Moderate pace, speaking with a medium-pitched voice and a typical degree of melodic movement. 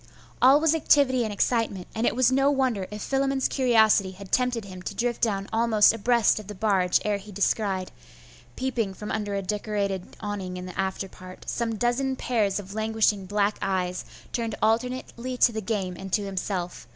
No: average, 180 wpm; high, 210 Hz; average, 3.7 semitones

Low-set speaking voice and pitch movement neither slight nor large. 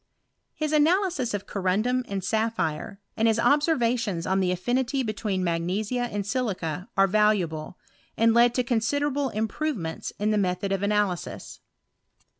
No: high, 215 Hz; average, 4.7 semitones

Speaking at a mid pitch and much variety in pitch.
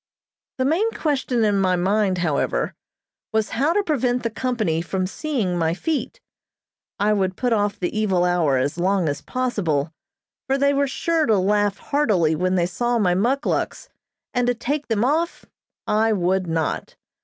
No: high, 210 Hz; wide, 6.1 semitones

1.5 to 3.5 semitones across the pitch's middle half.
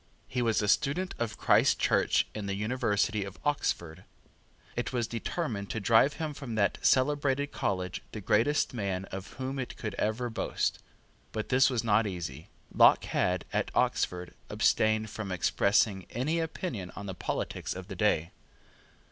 No: average, 4.7 semitones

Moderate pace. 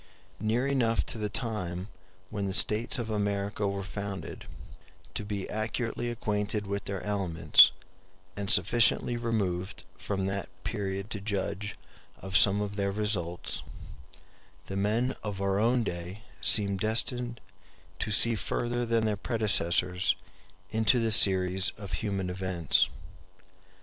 No: slow, 130 wpm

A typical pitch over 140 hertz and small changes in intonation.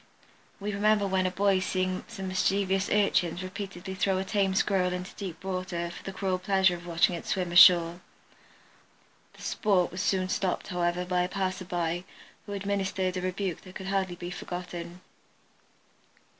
Yes: medium, 185 Hz; narrow, 1.5 semitones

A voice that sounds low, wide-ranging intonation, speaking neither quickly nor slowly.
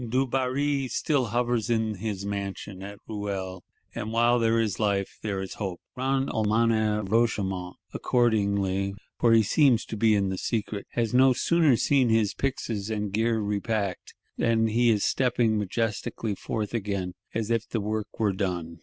No: low, 110 Hz; average, 2.8 semitones; average, 165 wpm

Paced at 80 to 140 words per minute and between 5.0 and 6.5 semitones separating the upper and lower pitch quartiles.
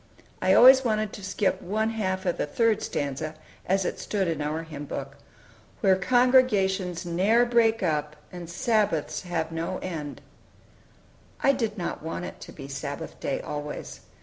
No: average, 160 wpm; average, 5.3 semitones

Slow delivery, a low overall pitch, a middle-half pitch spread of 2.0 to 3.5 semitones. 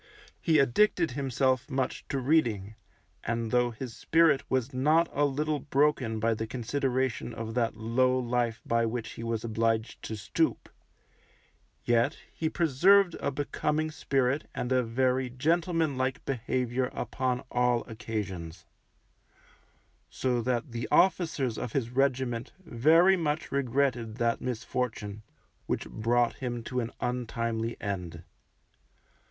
Yes: slow, 130 wpm; low, 125 Hz; average, 3.2 semitones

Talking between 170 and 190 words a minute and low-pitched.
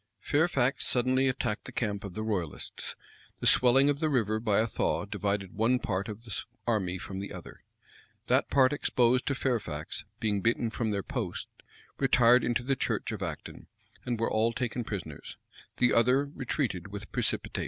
Yes: average, 175 wpm; low, 115 Hz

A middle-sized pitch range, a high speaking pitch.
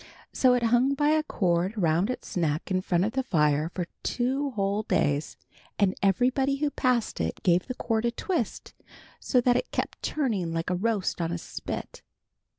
No: wide, 6.5 semitones; high, 215 Hz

